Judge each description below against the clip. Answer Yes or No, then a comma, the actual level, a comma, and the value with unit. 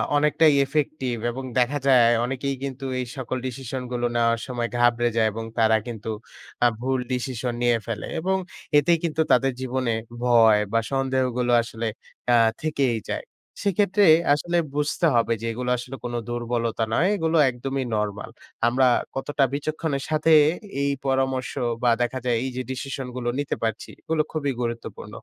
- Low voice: Yes, low, 130 Hz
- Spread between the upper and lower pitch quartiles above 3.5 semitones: No, average, 2.8 semitones